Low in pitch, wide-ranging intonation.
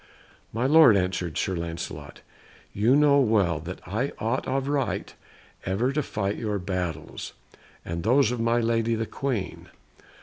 Yes: low, 110 Hz; wide, 6.0 semitones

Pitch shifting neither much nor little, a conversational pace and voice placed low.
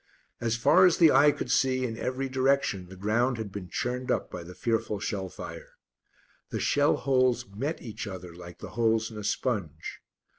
Yes: average, 4.6 semitones; average, 190 wpm; low, 115 Hz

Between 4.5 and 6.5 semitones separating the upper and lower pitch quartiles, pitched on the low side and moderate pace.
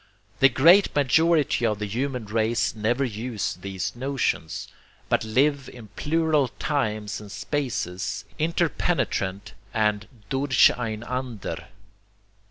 No: average, 4.9 semitones; low, 120 Hz; slow, 100 wpm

